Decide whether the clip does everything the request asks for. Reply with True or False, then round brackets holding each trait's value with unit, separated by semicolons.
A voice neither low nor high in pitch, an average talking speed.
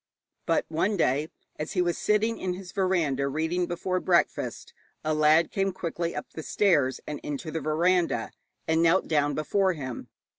True (165 Hz; 165 wpm)